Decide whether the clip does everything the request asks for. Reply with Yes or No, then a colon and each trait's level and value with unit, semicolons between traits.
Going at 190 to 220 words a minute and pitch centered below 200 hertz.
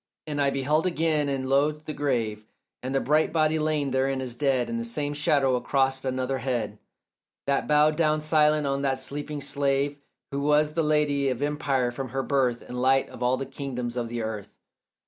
Yes: average, 195 wpm; low, 135 Hz